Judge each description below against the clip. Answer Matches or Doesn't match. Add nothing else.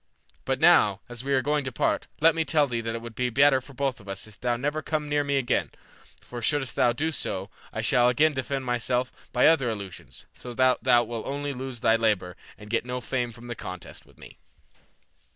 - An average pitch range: Matches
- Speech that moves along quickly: Matches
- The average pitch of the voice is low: Matches